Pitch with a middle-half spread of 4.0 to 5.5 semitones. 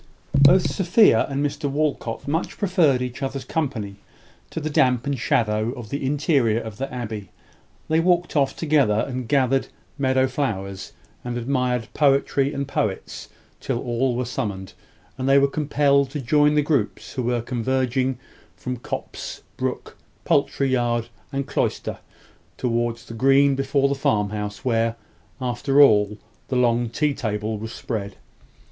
No: average, 3.3 semitones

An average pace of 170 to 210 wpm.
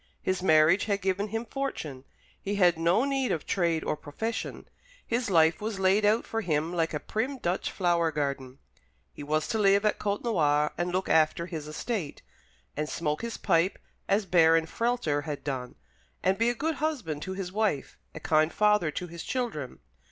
Yes: average, 180 wpm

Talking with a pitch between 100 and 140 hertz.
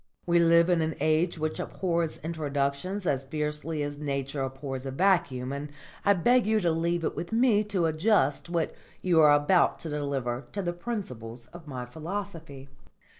No: medium, 160 Hz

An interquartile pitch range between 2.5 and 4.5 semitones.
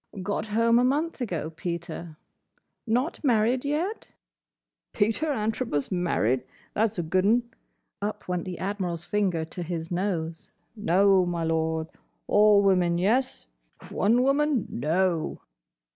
No: average, 5.2 semitones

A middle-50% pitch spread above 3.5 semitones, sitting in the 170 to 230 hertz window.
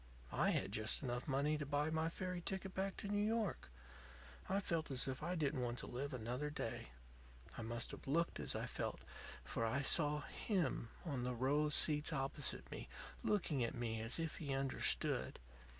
No: average, 4.7 semitones; medium, 145 Hz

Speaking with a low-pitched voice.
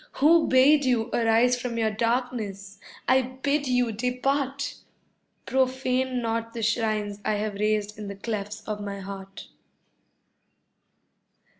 No: high, 230 Hz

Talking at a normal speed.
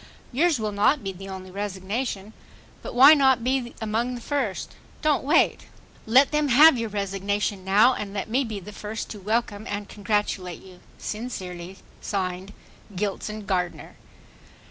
Yes: average, 150 wpm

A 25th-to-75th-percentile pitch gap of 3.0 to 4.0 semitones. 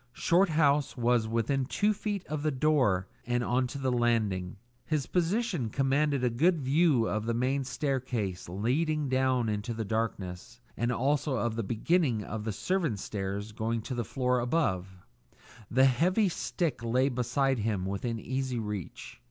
No: average, 4.5 semitones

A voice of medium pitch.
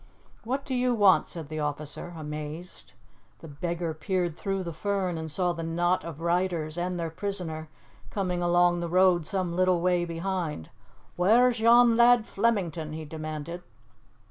Yes: medium, 175 Hz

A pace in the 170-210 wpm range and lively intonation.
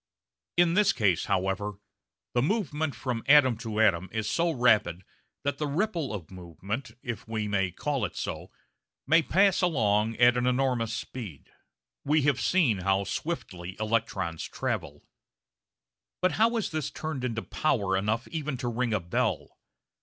No: average, 155 wpm; wide, 6.4 semitones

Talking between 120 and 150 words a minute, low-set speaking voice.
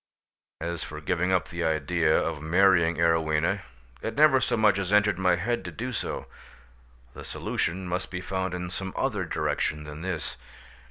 No: average, 170 wpm; very low, 90 Hz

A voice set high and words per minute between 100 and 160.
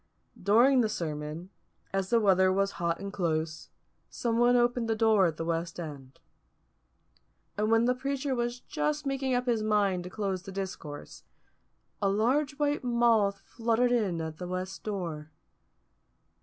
Yes: high, 205 Hz; average, 155 wpm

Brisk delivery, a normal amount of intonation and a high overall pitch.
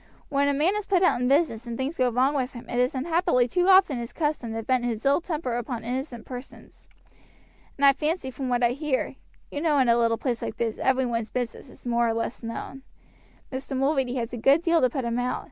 Yes: fast, 240 wpm; average, 3.3 semitones; very high, 255 Hz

